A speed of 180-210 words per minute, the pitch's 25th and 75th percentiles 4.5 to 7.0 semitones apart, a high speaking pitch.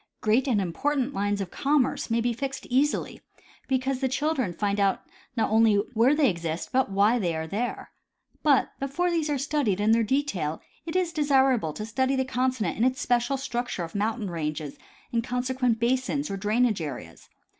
Yes: average, 185 wpm; average, 4.8 semitones; high, 240 Hz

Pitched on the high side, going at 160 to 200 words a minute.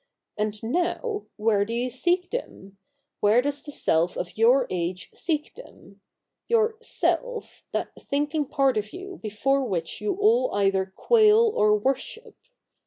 No: very high, 270 Hz; average, 150 wpm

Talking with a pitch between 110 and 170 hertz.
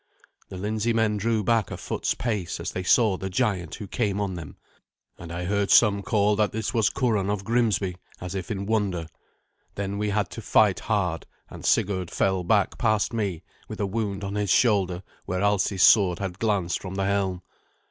No: low, 100 Hz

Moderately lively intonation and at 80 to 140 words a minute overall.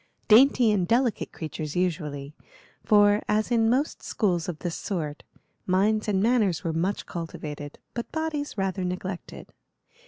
Yes: average, 5.0 semitones; slow, 135 wpm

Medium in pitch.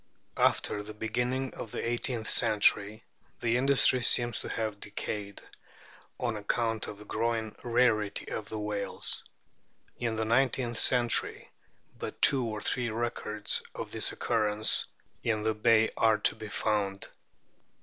No: low, 110 Hz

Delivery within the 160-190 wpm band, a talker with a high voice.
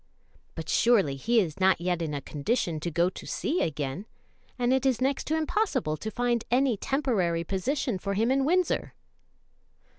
Yes: average, 175 wpm; high, 220 Hz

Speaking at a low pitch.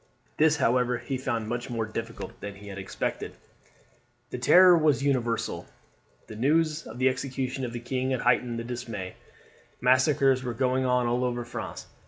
Yes: low, 125 Hz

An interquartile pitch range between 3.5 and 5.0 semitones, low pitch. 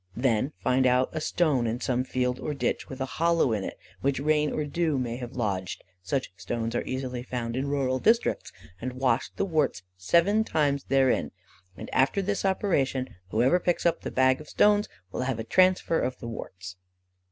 Yes: average, 4.0 semitones; low, 130 Hz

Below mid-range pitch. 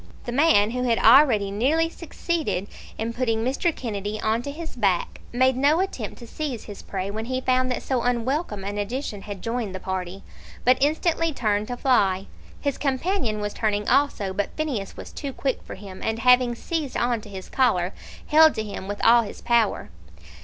No: high, 235 Hz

